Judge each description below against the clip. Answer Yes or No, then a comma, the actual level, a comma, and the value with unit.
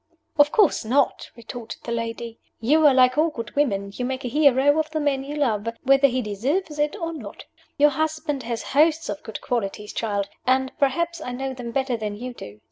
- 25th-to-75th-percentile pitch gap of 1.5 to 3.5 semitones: No, average, 4.3 semitones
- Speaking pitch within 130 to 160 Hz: No, very high, 260 Hz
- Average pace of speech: No, fast, 210 wpm